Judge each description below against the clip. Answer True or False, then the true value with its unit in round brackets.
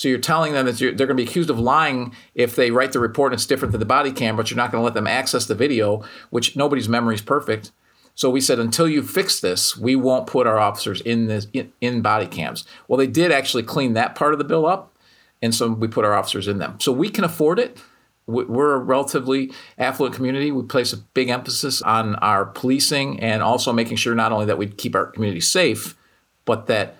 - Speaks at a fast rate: True (240 wpm)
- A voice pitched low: True (125 Hz)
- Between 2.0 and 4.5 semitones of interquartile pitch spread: True (3.1 semitones)